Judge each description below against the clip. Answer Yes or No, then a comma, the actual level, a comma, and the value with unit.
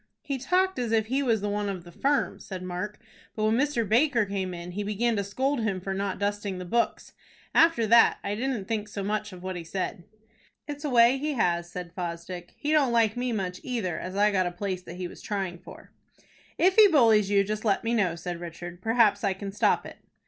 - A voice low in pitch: No, high, 205 Hz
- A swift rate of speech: Yes, fast, 230 wpm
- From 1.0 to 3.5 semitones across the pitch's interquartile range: No, average, 4.3 semitones